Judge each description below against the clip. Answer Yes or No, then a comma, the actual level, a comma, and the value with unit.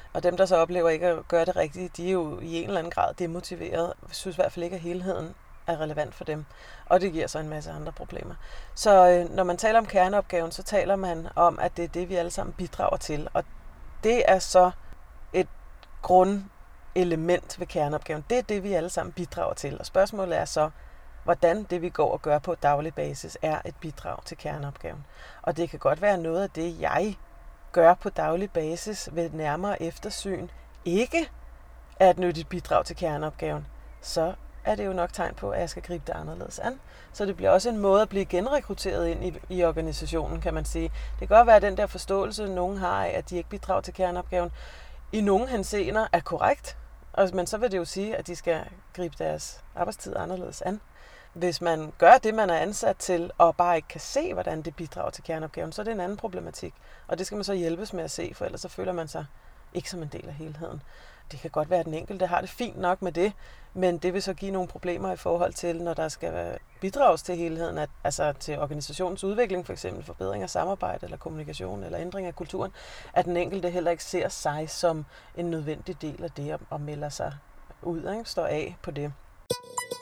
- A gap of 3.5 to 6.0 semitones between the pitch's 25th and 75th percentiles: No, average, 2.8 semitones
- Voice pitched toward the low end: No, medium, 175 Hz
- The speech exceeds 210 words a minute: Yes, average, 220 wpm